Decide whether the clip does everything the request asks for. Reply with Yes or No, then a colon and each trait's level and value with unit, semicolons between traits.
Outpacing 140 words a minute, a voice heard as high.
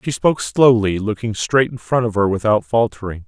No: average, 200 wpm; low, 110 Hz